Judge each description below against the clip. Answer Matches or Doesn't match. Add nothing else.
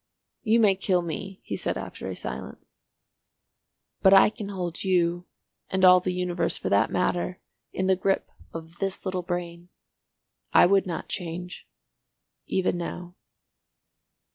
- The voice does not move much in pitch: Matches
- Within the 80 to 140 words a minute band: Matches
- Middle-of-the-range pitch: Matches